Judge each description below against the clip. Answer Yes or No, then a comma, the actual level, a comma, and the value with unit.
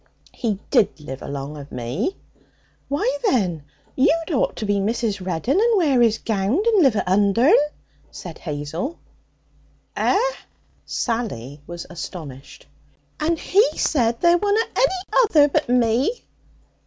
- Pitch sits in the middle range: No, high, 235 Hz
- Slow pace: Yes, slow, 130 wpm